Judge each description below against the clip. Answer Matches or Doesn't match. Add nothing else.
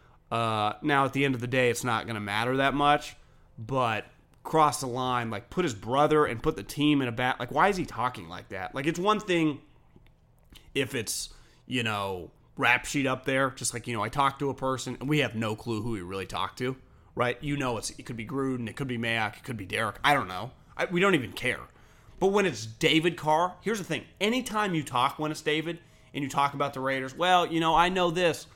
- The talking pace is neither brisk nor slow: Doesn't match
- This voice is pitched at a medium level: Doesn't match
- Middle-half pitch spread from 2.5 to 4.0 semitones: Doesn't match